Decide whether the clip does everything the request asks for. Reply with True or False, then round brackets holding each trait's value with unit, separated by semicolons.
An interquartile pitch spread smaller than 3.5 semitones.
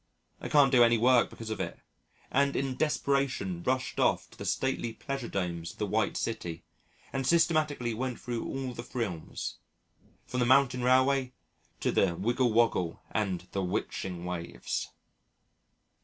False (5.4 semitones)